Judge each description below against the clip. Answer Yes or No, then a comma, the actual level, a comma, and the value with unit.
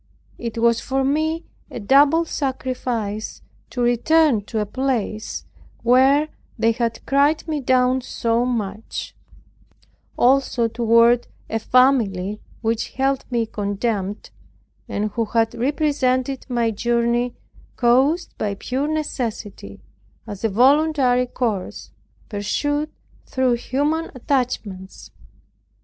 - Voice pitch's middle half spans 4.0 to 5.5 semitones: No, average, 3.3 semitones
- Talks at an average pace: No, slow, 110 wpm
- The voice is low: No, high, 245 Hz